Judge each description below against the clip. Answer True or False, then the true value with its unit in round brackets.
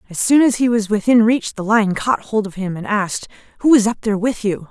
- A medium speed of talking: False (270 wpm)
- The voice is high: True (215 Hz)